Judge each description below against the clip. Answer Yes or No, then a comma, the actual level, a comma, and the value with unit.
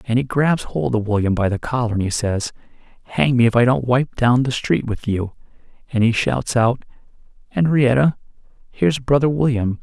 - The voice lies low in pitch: Yes, low, 120 Hz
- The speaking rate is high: No, average, 190 wpm